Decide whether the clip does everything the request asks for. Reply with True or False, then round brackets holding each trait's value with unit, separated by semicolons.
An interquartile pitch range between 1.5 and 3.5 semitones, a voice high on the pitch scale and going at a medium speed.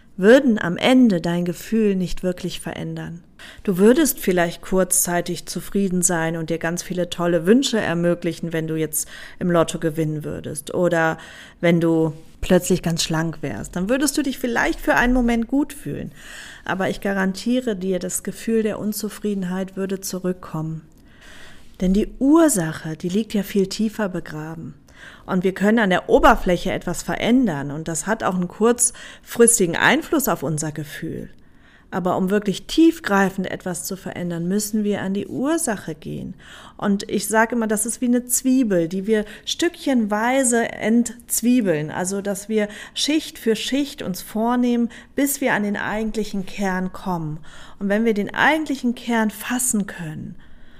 False (5.0 semitones; 195 Hz; 155 wpm)